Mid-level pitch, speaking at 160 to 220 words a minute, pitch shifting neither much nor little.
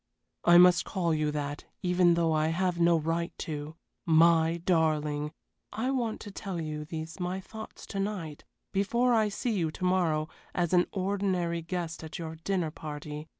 Yes: medium, 170 Hz; average, 170 wpm; average, 3.1 semitones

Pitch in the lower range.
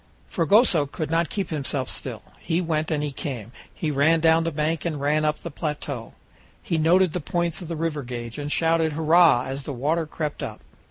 No: medium, 155 Hz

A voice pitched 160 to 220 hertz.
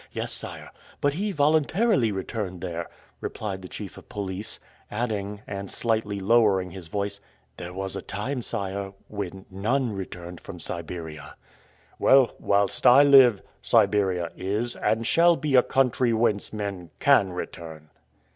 No: low, 100 Hz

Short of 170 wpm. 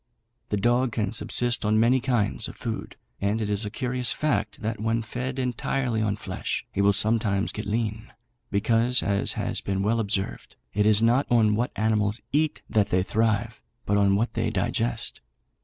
No: average, 180 wpm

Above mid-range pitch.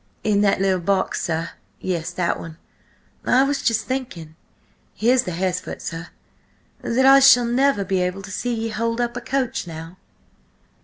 Yes: high, 200 Hz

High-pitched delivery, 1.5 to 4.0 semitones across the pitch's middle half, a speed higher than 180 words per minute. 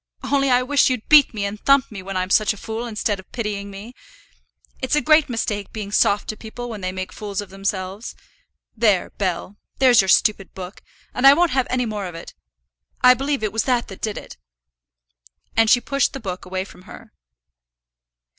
No: high, 215 Hz; average, 4.4 semitones; average, 200 wpm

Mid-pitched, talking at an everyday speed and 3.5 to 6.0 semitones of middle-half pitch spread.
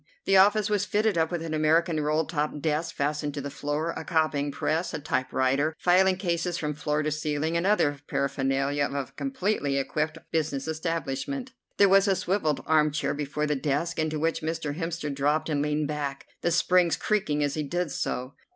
No: medium, 155 Hz; average, 190 wpm; average, 2.8 semitones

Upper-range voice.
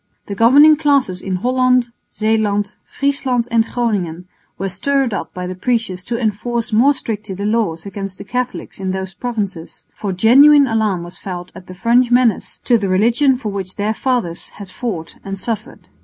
Yes: high, 215 Hz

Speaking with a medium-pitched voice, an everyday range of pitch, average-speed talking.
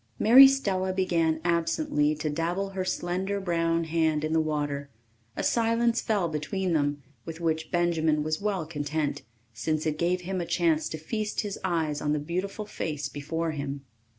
Yes: medium, 165 Hz; average, 3.5 semitones; average, 170 wpm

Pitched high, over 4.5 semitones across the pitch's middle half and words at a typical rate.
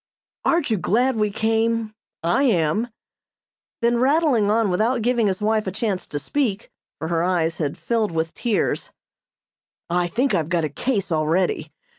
Yes: high, 210 Hz; wide, 5.4 semitones; average, 160 wpm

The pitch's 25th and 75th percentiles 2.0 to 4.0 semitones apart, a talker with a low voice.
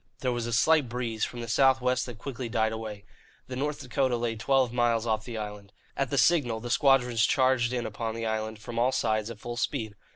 Yes: narrow, 2.4 semitones; low, 120 Hz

